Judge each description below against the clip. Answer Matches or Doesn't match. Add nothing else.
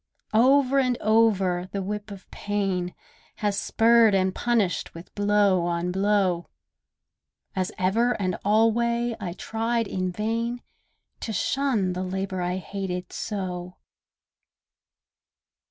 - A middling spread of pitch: Matches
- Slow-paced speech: Matches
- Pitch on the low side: Doesn't match